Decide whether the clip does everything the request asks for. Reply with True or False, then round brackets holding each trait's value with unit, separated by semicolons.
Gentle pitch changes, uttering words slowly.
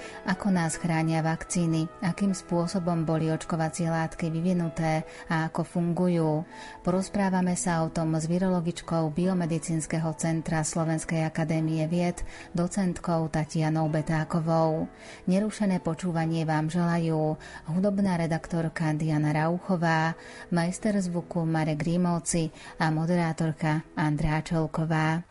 True (1.7 semitones; 100 wpm)